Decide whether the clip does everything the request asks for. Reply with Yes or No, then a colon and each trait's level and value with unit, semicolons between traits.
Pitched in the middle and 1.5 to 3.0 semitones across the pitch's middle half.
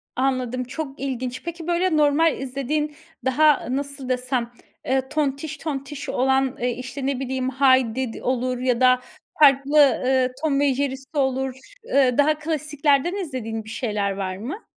No: very high, 265 Hz; narrow, 2.4 semitones